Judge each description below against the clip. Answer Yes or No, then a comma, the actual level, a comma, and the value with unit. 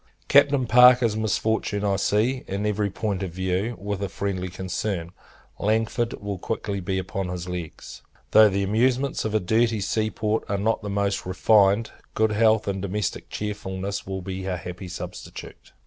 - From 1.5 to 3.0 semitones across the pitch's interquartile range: Yes, narrow, 2.5 semitones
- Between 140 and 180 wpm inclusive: Yes, average, 165 wpm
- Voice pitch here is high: No, low, 100 Hz